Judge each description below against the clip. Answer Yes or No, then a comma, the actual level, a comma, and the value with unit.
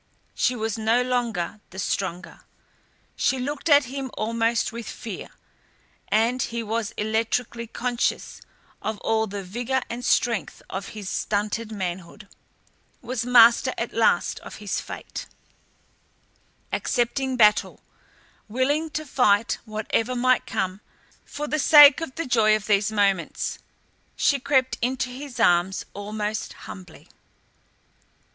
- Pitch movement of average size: Yes, average, 3.3 semitones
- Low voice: No, high, 230 Hz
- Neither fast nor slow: No, slow, 125 wpm